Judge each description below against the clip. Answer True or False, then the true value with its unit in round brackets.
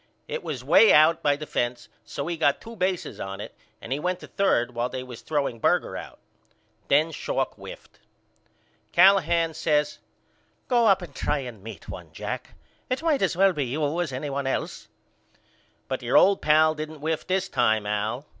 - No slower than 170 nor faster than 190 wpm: True (185 wpm)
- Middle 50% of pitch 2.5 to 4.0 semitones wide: False (5.6 semitones)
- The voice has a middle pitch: True (150 Hz)